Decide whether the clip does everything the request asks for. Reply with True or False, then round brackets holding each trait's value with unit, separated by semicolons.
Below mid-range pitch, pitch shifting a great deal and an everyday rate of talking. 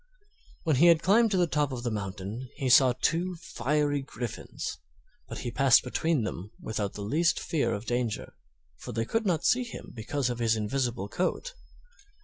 True (130 Hz; 6.6 semitones; 180 wpm)